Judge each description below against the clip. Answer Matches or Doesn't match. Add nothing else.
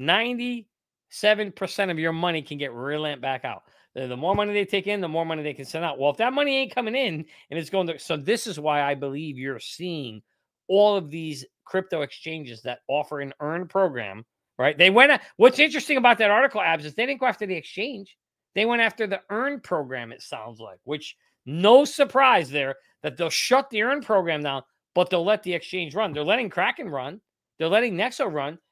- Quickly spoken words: Matches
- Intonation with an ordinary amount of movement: Doesn't match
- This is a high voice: Doesn't match